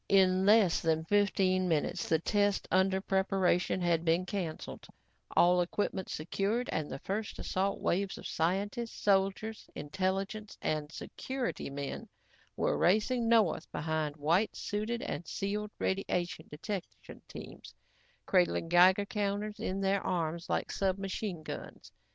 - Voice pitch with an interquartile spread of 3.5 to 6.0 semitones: No, average, 3.0 semitones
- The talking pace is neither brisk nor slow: No, slow, 125 wpm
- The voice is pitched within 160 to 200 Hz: Yes, high, 190 Hz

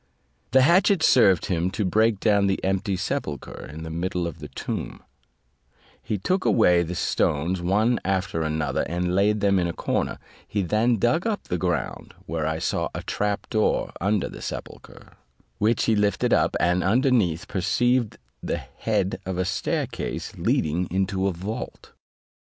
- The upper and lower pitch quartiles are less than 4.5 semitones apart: Yes, average, 3.6 semitones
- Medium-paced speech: Yes, average, 165 wpm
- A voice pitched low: Yes, very low, 95 Hz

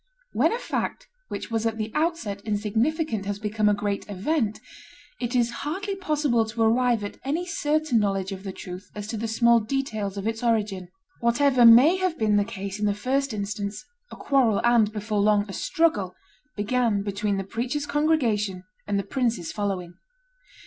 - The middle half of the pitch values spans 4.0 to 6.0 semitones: Yes, average, 4.4 semitones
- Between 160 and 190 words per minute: Yes, average, 175 wpm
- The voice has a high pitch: Yes, high, 220 Hz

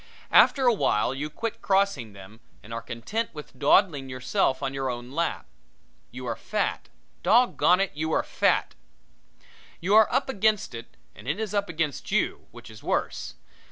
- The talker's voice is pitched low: No, medium, 150 Hz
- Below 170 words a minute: No, average, 175 wpm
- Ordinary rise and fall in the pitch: No, wide, 8.0 semitones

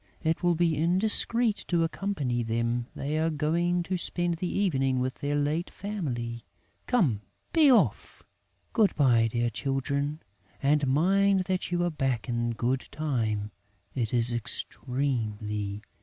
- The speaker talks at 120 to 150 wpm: Yes, average, 140 wpm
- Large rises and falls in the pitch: Yes, wide, 6.6 semitones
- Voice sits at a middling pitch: Yes, medium, 145 Hz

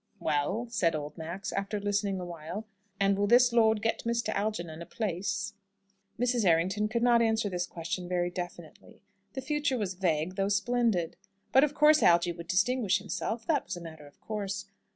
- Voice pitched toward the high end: Yes, high, 200 Hz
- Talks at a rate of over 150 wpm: Yes, average, 175 wpm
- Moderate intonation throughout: Yes, average, 4.7 semitones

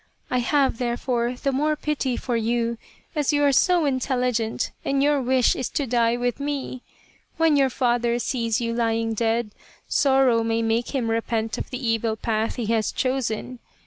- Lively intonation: No, average, 2.8 semitones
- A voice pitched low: No, high, 245 Hz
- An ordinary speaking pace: Yes, average, 175 wpm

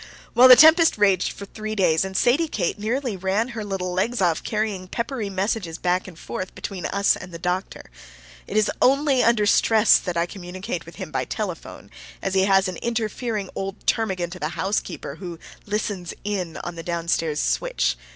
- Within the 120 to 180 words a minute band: No, average, 190 wpm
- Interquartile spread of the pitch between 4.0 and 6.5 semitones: No, average, 3.5 semitones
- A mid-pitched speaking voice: No, high, 195 Hz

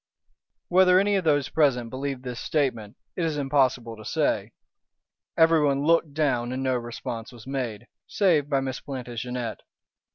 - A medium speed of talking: Yes, average, 150 wpm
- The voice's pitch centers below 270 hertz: Yes, low, 135 Hz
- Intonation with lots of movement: No, average, 3.7 semitones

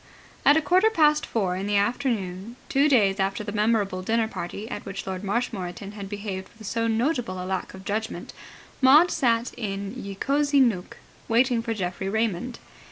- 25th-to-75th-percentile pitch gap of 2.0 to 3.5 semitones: No, average, 4.0 semitones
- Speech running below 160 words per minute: No, average, 175 wpm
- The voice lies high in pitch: Yes, high, 215 Hz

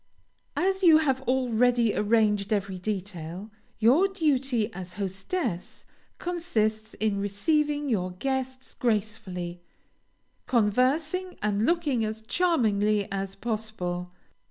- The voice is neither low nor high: No, high, 220 Hz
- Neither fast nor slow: No, slow, 100 wpm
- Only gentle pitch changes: No, average, 5.2 semitones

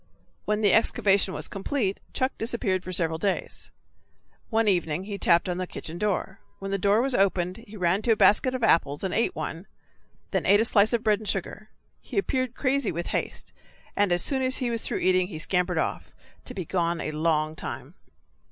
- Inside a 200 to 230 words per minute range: Yes, fast, 205 wpm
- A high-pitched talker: Yes, high, 195 Hz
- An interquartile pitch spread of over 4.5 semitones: No, average, 4.0 semitones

